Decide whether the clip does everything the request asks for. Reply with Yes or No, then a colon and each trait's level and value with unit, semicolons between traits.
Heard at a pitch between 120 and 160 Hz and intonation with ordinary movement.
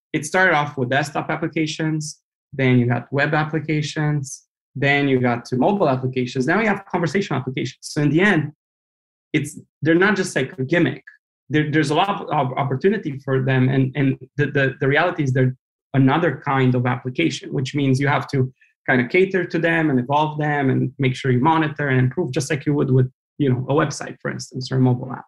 Yes: medium, 140 Hz; average, 3.3 semitones